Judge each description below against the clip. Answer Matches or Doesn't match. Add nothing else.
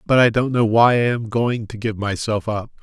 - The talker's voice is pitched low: Matches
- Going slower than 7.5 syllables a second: Matches